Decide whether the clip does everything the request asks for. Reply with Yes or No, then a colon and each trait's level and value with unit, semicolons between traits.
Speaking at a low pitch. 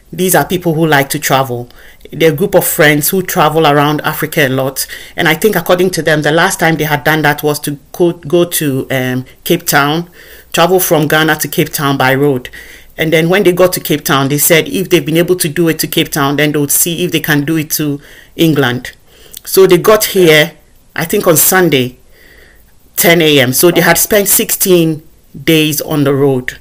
No: medium, 155 Hz